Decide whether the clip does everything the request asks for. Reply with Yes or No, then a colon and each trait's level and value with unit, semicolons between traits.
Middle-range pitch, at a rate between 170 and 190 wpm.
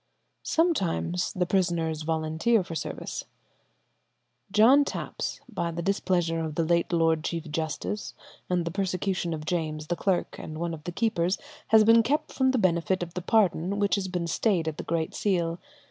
Yes: medium, 175 Hz; average, 175 wpm